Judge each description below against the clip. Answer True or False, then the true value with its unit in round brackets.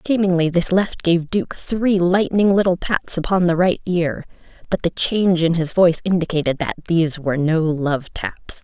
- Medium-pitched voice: True (175 Hz)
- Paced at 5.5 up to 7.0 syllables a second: False (4.9 syllables/s)